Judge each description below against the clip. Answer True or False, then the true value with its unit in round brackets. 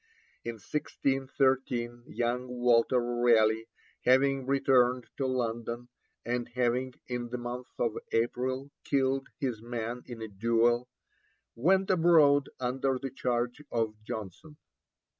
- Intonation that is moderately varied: False (2.1 semitones)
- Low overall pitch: True (125 Hz)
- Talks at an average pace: False (115 wpm)